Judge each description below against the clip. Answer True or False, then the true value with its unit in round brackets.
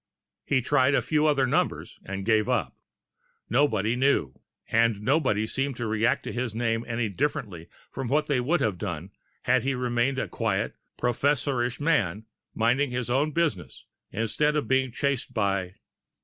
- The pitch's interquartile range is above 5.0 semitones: False (4.1 semitones)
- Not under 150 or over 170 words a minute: True (160 wpm)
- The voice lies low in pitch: True (120 Hz)